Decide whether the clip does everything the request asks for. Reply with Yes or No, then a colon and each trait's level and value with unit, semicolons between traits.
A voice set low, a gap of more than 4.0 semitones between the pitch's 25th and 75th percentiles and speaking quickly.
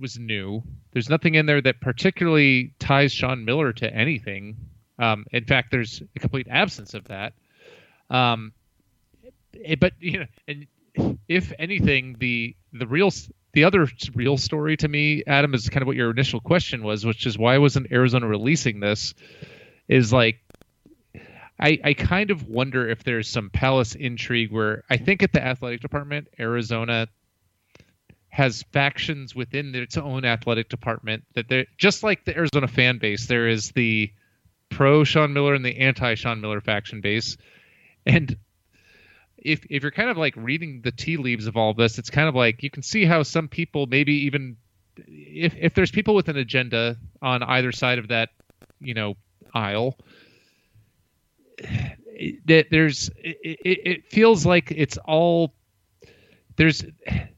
No: low, 125 Hz; average, 4.5 semitones; average, 160 wpm